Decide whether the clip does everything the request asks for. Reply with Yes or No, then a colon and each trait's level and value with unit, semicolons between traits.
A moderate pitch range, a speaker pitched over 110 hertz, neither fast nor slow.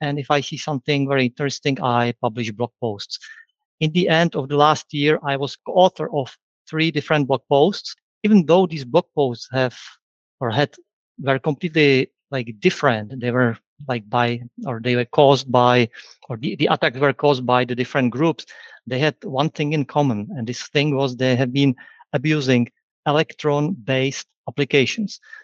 Yes: average, 3.5 semitones; medium, 140 Hz; average, 170 wpm